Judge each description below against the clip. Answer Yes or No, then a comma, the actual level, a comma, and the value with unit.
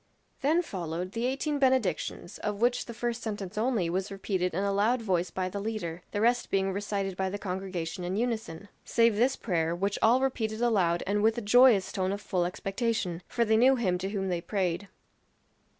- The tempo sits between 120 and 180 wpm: No, average, 200 wpm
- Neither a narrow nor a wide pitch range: Yes, average, 4.0 semitones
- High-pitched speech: Yes, high, 200 Hz